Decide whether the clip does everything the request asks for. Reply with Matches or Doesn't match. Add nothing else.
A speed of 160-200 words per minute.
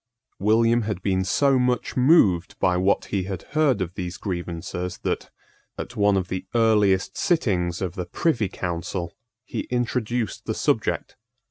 Doesn't match